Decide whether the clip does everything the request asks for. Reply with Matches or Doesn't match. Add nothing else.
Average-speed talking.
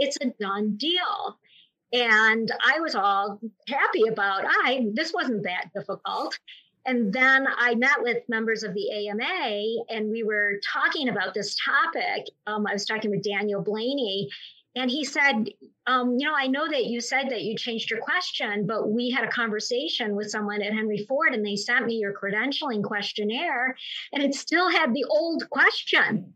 Matches